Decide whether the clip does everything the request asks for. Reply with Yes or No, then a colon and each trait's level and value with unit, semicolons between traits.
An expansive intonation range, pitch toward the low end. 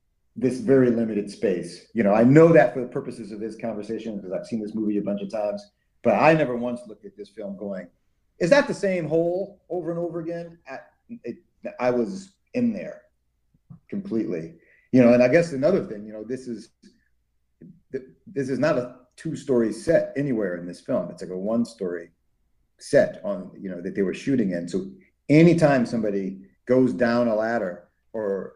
Yes: wide, 7.2 semitones; low, 125 Hz